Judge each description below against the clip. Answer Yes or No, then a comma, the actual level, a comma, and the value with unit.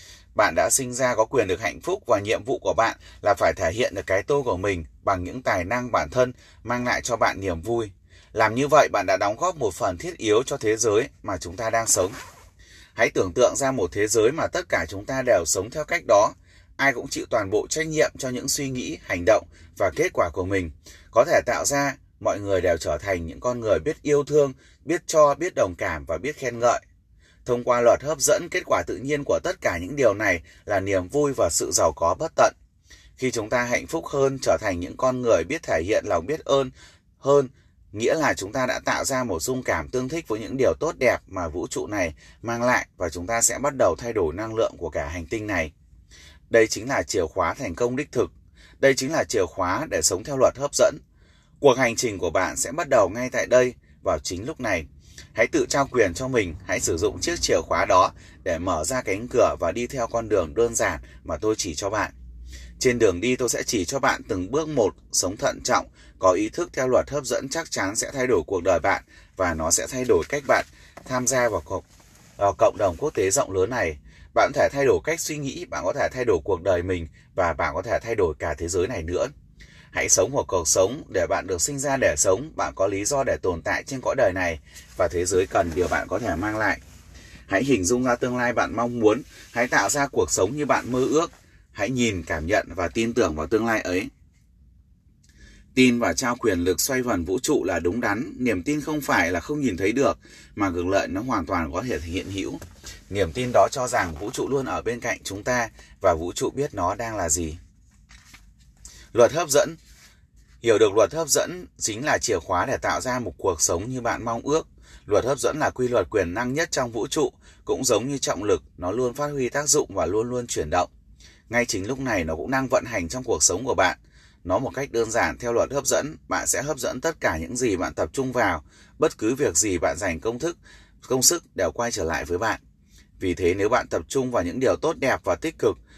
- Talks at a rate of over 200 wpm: Yes, average, 245 wpm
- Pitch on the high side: No, low, 120 Hz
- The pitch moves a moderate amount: No, wide, 7.3 semitones